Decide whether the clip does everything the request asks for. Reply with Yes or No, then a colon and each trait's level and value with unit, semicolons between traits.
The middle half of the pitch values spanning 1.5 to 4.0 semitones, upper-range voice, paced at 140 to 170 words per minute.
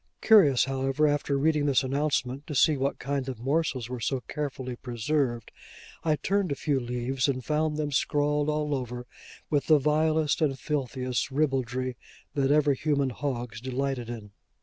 No: average, 2.8 semitones; medium, 140 Hz; average, 165 wpm